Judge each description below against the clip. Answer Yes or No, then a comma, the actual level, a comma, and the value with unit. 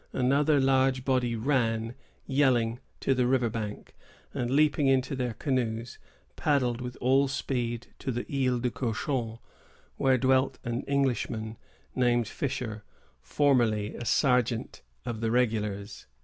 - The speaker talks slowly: Yes, slow, 130 wpm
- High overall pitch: No, low, 125 Hz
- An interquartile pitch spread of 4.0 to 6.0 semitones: No, narrow, 2.6 semitones